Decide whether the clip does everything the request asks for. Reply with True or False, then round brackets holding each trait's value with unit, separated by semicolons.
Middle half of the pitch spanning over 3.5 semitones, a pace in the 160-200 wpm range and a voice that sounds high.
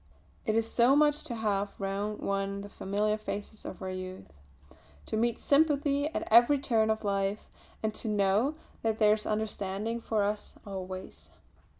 False (2.7 semitones; 165 wpm; 215 Hz)